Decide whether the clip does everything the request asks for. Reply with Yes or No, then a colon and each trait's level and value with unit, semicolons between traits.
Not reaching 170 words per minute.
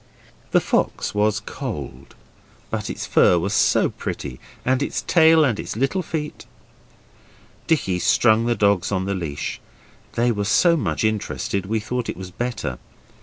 Yes: average, 155 wpm